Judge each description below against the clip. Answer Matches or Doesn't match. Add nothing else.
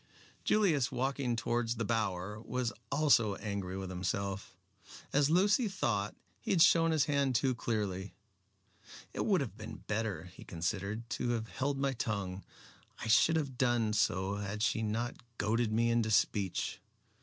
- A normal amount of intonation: Matches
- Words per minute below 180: Matches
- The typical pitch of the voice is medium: Doesn't match